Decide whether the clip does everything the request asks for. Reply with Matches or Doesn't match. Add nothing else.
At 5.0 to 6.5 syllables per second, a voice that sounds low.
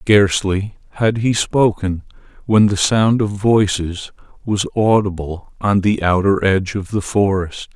Doesn't match